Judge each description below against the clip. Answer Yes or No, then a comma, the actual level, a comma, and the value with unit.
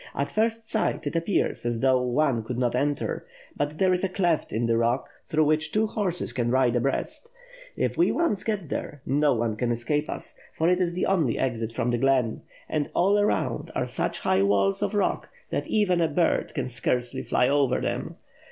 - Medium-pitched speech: Yes, medium, 145 Hz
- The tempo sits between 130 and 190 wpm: No, fast, 205 wpm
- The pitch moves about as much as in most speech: No, wide, 6.8 semitones